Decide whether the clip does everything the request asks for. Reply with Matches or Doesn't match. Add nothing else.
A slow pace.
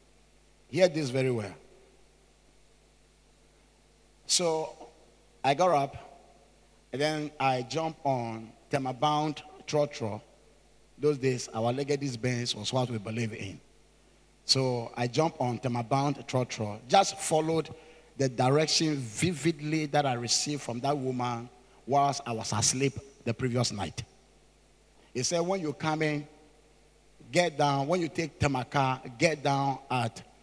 Matches